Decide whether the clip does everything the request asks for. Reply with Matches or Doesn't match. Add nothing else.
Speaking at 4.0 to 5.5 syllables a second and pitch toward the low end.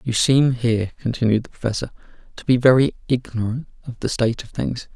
Doesn't match